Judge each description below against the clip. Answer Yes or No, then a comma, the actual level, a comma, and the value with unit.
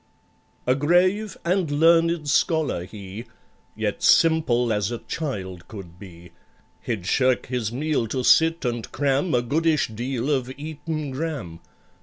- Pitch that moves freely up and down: Yes, wide, 6.0 semitones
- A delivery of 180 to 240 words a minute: No, slow, 135 wpm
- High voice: No, low, 135 Hz